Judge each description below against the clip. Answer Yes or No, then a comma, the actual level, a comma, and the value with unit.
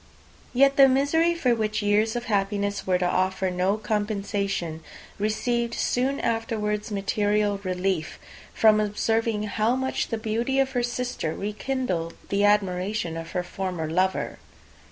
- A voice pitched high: Yes, high, 210 Hz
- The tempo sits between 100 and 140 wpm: Yes, slow, 135 wpm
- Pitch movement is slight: No, average, 3.5 semitones